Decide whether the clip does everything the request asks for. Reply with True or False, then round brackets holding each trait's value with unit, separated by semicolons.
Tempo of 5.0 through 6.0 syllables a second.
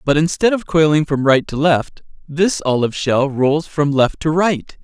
False (4.5 syllables/s)